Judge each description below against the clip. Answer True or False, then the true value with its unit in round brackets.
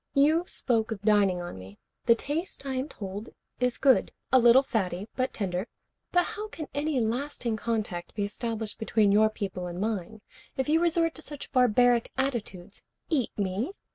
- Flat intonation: False (5.1 semitones)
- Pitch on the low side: False (230 Hz)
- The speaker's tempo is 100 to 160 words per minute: False (170 wpm)